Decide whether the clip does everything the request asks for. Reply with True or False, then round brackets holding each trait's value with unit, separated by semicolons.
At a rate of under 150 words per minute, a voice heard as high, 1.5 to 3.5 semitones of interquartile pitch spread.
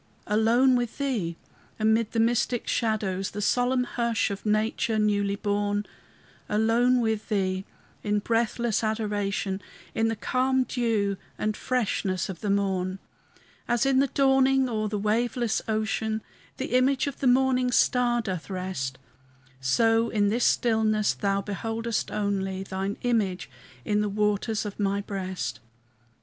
True (135 wpm; 215 Hz; 3.0 semitones)